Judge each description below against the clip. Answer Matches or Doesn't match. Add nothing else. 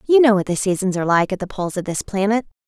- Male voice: Doesn't match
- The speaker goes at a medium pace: Doesn't match